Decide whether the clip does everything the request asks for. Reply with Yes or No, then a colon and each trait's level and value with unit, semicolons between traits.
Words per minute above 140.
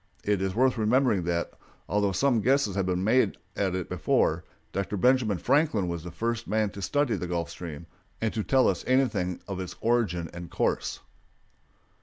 Yes: average, 180 wpm